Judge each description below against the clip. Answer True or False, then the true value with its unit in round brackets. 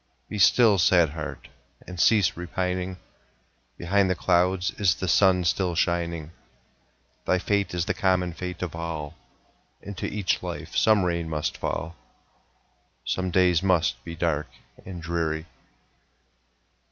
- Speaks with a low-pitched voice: True (90 Hz)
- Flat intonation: True (1.9 semitones)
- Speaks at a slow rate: True (130 wpm)